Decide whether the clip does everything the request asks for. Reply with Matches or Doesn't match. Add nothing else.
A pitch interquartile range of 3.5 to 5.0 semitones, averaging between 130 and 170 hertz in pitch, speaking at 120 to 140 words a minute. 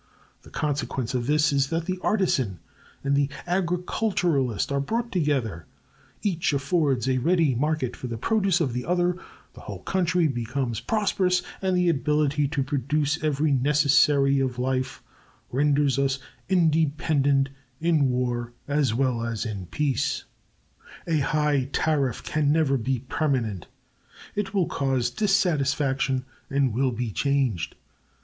Matches